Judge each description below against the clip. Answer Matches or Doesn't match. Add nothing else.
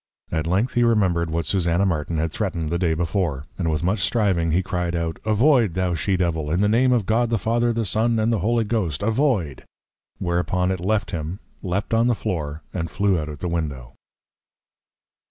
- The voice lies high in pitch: Doesn't match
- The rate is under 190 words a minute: Doesn't match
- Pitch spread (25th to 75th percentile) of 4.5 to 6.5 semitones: Matches